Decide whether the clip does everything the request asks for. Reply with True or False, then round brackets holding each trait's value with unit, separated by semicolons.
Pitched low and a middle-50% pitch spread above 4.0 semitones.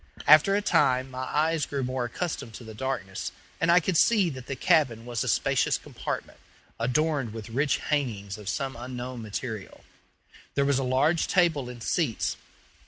True (130 Hz; 4.4 semitones)